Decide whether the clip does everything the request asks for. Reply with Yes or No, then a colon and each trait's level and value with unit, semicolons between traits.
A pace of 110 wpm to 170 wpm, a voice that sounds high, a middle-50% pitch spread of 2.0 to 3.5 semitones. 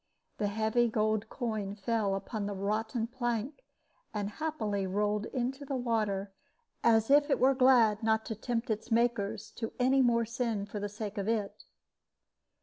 Yes: average, 160 wpm; high, 220 Hz; average, 2.7 semitones